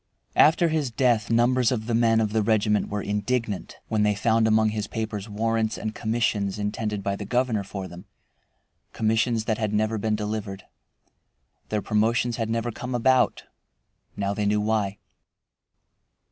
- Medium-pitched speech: No, low, 110 Hz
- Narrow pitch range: Yes, narrow, 1.8 semitones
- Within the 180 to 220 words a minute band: No, average, 160 wpm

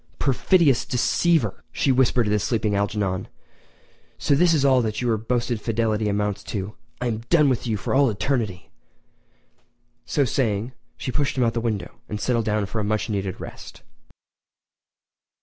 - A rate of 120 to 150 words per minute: No, average, 165 wpm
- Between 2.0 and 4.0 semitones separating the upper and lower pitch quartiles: Yes, average, 3.7 semitones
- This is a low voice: Yes, low, 115 Hz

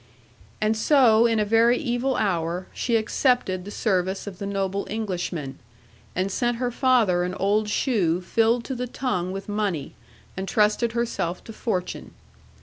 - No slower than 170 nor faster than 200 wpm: No, average, 155 wpm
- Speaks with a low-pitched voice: No, high, 210 Hz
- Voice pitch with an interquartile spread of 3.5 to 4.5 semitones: Yes, average, 4.1 semitones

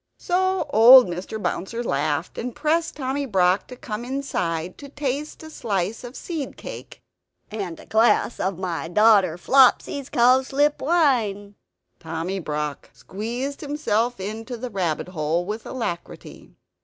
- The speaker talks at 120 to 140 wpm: Yes, slow, 135 wpm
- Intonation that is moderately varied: No, wide, 6.7 semitones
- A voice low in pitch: No, high, 225 Hz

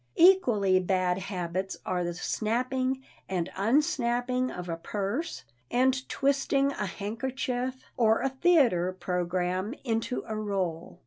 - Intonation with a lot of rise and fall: Yes, wide, 5.8 semitones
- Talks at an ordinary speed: No, slow, 120 wpm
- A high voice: Yes, high, 220 Hz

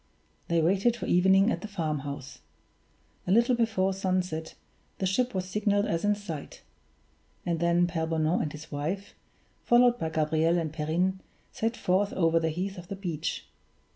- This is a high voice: No, medium, 180 Hz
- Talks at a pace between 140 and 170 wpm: Yes, average, 165 wpm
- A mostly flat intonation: No, average, 3.7 semitones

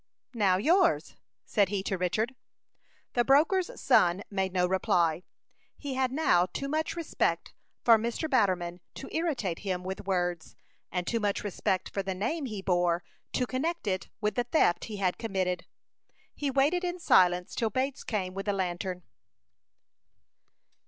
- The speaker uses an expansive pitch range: Yes, wide, 6.4 semitones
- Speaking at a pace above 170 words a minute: No, average, 155 wpm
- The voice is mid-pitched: No, high, 200 Hz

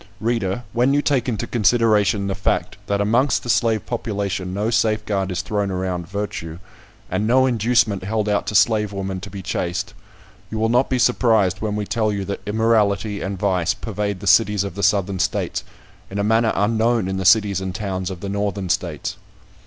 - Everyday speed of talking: Yes, average, 190 wpm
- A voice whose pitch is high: No, low, 105 Hz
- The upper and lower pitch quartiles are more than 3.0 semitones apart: No, narrow, 2.5 semitones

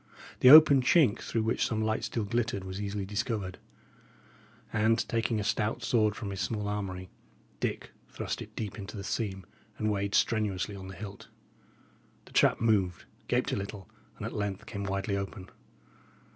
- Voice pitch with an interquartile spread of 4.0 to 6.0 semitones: No, narrow, 2.4 semitones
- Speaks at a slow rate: No, average, 170 wpm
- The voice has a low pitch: Yes, low, 105 Hz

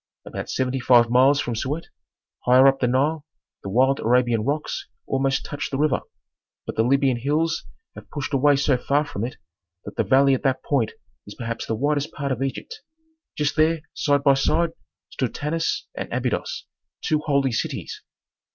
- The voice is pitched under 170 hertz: Yes, low, 135 Hz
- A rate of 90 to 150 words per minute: No, average, 175 wpm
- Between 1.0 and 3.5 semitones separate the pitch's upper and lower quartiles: Yes, narrow, 2.6 semitones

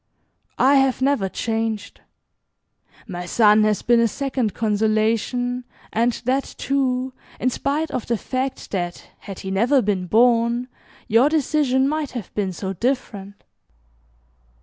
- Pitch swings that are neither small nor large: Yes, average, 3.8 semitones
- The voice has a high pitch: Yes, high, 235 Hz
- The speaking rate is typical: No, slow, 130 wpm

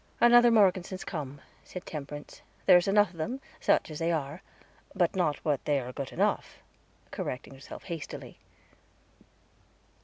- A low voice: No, medium, 165 Hz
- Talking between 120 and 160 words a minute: Yes, average, 140 wpm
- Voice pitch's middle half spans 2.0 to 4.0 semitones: No, average, 4.8 semitones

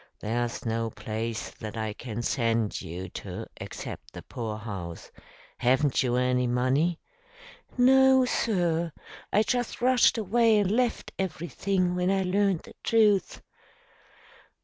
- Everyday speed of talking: No, slow, 125 wpm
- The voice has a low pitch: No, medium, 155 Hz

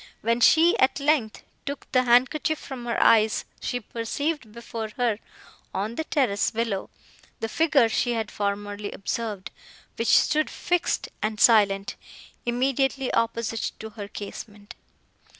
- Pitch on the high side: Yes, high, 230 Hz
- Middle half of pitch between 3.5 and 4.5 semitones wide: Yes, average, 3.9 semitones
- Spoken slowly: Yes, slow, 130 wpm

